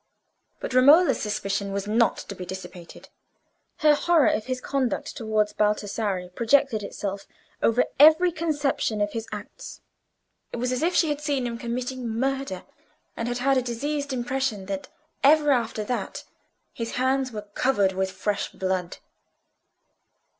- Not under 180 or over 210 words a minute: No, average, 145 wpm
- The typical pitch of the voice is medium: No, high, 240 Hz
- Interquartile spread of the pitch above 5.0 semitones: No, average, 4.7 semitones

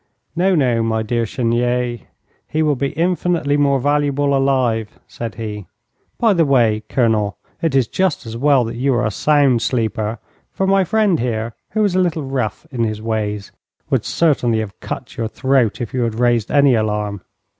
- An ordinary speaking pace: Yes, average, 180 wpm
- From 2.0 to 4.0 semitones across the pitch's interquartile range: No, average, 4.5 semitones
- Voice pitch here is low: Yes, low, 125 Hz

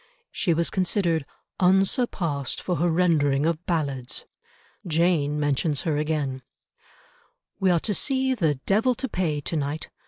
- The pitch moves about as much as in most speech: Yes, average, 4.1 semitones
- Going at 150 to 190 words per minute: No, slow, 135 wpm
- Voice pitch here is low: No, medium, 165 Hz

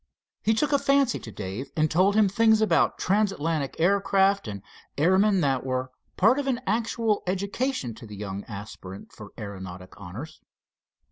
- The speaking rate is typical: Yes, average, 155 wpm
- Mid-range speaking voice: Yes, medium, 175 Hz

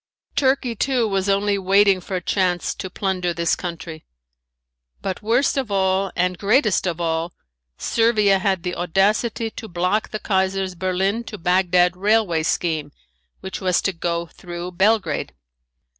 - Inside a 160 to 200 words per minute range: No, average, 145 wpm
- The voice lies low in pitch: No, high, 190 Hz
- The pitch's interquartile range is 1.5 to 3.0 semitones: Yes, average, 2.7 semitones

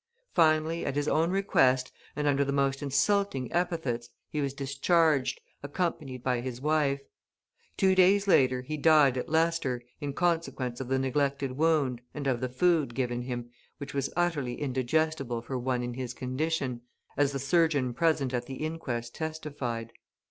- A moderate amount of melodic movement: Yes, average, 3.7 semitones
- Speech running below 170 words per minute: Yes, average, 160 wpm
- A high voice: No, medium, 140 Hz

